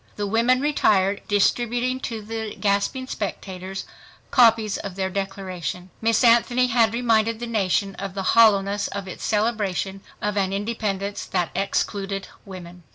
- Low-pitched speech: No, high, 205 Hz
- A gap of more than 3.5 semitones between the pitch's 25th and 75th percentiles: No, average, 2.8 semitones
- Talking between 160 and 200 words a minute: No, average, 140 wpm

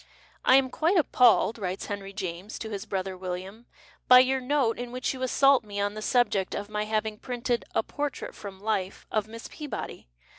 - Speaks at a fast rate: Yes, fast, 215 wpm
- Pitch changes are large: No, average, 4.0 semitones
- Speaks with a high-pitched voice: Yes, high, 220 Hz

